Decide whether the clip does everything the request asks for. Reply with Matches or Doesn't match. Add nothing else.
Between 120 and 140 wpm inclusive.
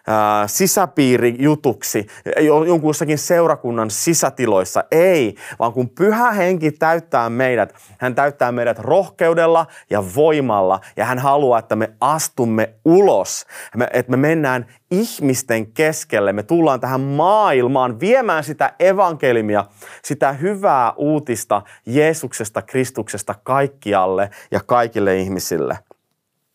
Doesn't match